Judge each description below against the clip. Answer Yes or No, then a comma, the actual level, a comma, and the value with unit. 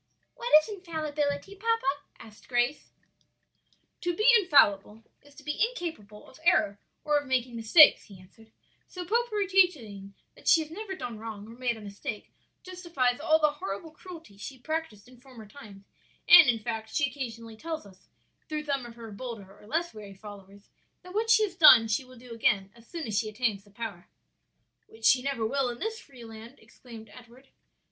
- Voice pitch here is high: Yes, very high, 250 Hz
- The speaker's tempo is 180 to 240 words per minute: Yes, average, 185 wpm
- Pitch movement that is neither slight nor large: No, wide, 6.4 semitones